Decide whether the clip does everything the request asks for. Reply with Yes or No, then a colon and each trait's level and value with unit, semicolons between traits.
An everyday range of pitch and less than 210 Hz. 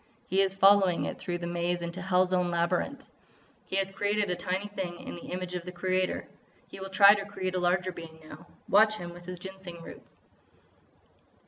No: narrow, 1.8 semitones; medium, 185 Hz